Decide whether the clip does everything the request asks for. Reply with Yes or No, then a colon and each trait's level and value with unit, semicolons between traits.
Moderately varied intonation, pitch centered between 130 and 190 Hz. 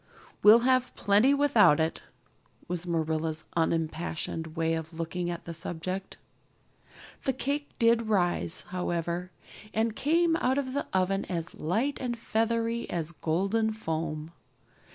No: wide, 6.0 semitones; medium, 185 Hz